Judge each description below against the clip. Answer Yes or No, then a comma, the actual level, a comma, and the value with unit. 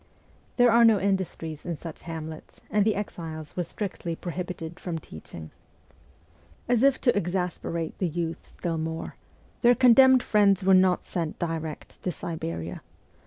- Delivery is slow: No, average, 165 wpm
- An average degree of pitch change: Yes, average, 3.9 semitones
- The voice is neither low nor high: Yes, medium, 175 Hz